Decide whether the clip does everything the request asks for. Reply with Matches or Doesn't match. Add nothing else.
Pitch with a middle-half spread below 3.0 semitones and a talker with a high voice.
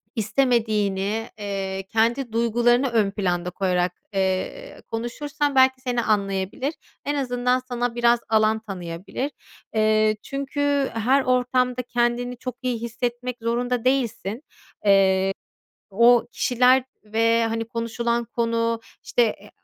Matches